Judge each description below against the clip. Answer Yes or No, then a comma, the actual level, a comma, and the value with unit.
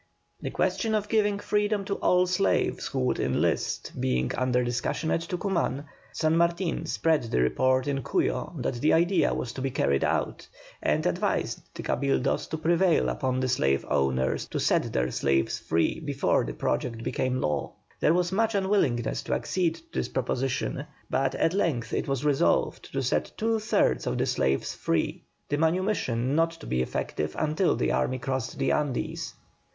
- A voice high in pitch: No, medium, 140 Hz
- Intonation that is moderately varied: No, wide, 6.2 semitones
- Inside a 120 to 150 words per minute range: No, average, 170 wpm